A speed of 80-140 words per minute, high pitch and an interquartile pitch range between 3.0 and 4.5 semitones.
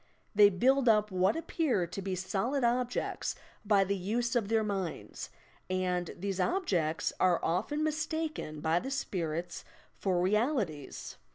No: slow, 135 wpm; high, 200 Hz; wide, 5.5 semitones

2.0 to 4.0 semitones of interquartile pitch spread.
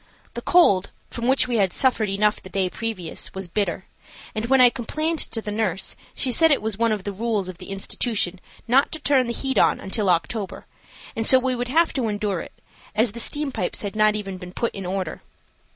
No: average, 4.4 semitones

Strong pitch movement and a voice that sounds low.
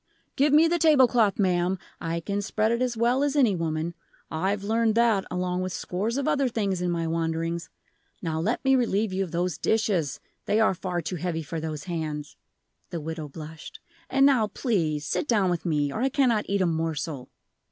No: wide, 5.7 semitones; medium, 185 Hz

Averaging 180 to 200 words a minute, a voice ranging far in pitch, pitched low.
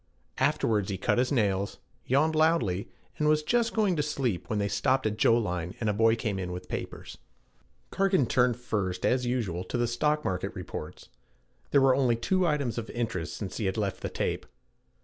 Yes: average, 190 wpm; wide, 5.8 semitones; low, 120 Hz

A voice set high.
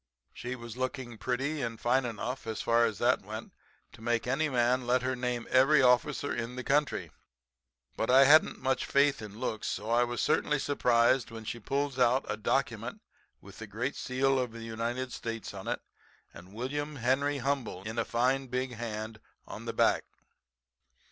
No: low, 125 Hz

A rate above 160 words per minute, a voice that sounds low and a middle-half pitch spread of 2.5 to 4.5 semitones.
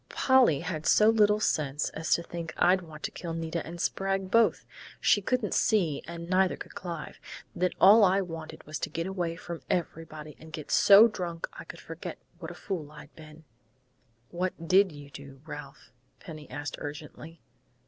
No: average, 180 wpm; medium, 165 Hz; average, 3.6 semitones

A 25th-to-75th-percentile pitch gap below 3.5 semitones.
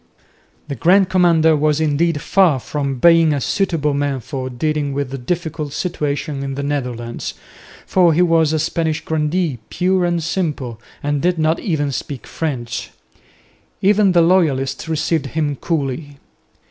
Yes: average, 3.1 semitones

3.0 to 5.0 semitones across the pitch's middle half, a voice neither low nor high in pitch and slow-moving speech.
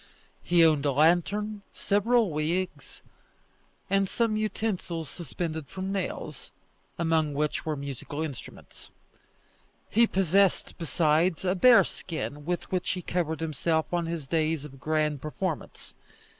Yes: average, 3.6 semitones; medium, 165 Hz; slow, 120 wpm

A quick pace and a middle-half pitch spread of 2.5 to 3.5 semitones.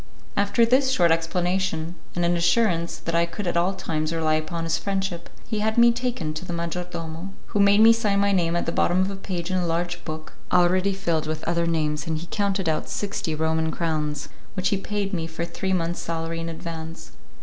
Yes: fast, 215 wpm; average, 2.9 semitones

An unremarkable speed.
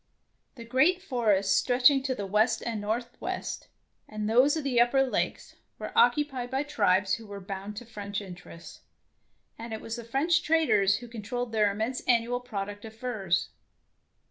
Yes: average, 170 wpm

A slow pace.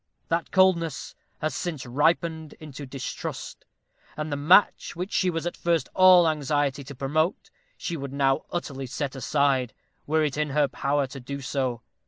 No: average, 165 wpm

